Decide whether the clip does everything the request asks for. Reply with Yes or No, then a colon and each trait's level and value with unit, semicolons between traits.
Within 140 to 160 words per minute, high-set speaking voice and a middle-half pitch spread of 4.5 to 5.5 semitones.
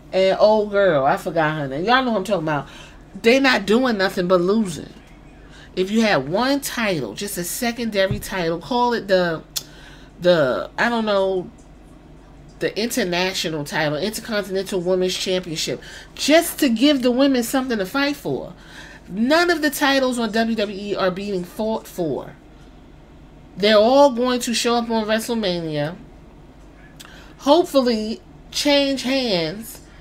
Yes: average, 145 wpm; high, 205 Hz; average, 5.0 semitones